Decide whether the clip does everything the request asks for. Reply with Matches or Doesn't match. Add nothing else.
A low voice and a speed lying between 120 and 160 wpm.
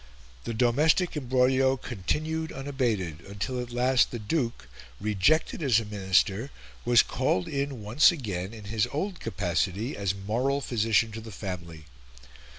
Matches